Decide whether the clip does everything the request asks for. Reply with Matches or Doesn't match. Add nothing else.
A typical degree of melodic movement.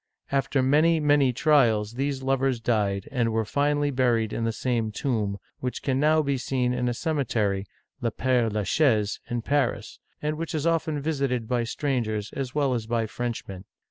Matches